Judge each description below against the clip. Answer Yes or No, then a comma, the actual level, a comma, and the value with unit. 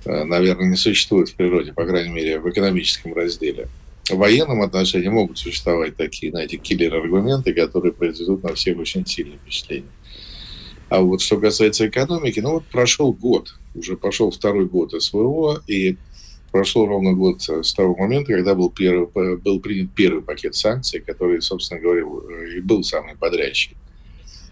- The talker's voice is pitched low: Yes, low, 100 Hz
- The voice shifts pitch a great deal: Yes, wide, 8.9 semitones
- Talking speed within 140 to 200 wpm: Yes, average, 150 wpm